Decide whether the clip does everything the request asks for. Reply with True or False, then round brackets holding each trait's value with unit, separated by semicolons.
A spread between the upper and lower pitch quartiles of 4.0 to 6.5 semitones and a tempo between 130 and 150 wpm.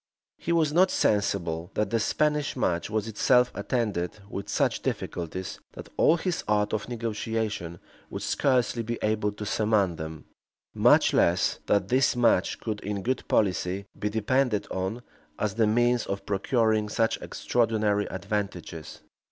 False (3.3 semitones; 145 wpm)